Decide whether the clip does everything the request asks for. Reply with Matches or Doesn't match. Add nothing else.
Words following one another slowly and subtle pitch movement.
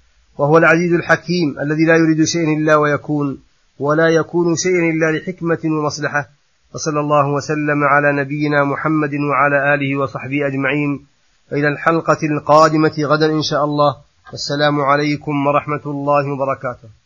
Doesn't match